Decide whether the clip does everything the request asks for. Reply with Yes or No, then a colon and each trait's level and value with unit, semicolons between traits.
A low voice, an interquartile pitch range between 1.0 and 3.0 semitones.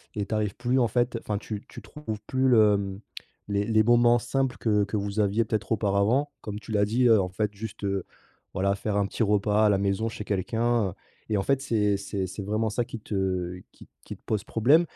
Yes: low, 105 Hz; narrow, 2.5 semitones